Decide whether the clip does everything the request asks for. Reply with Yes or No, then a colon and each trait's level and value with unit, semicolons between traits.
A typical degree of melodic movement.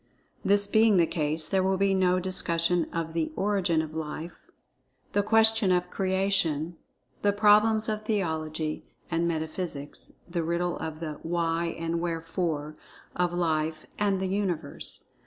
Yes: average, 3.2 semitones